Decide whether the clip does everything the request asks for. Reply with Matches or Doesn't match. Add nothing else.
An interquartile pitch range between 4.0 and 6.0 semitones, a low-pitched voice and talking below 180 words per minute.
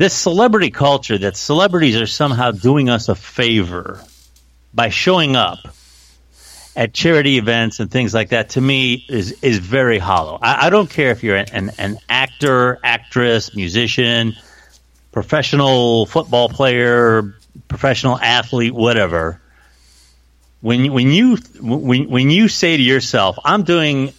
Matches